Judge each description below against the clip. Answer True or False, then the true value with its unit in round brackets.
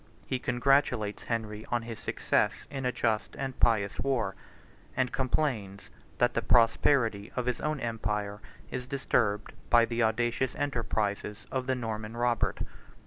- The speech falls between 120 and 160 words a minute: True (140 wpm)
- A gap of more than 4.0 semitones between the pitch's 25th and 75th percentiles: False (3.0 semitones)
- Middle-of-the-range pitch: False (115 Hz)